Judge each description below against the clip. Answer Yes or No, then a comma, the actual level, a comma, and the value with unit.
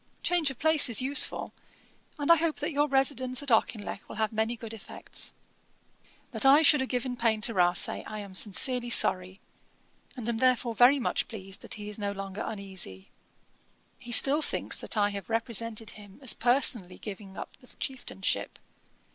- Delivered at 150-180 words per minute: Yes, average, 175 wpm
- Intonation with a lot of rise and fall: No, average, 4.3 semitones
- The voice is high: Yes, high, 230 Hz